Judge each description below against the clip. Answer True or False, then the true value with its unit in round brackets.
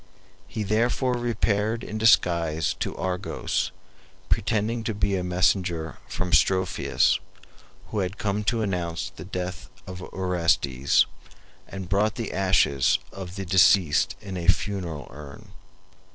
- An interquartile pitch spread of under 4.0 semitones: True (3.0 semitones)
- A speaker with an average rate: False (125 wpm)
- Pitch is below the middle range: True (95 Hz)